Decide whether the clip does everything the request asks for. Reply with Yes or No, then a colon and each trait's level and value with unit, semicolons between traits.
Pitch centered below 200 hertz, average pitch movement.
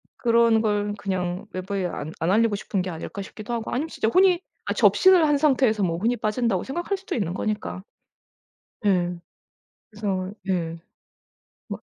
No: high, 210 Hz; average, 4.4 semitones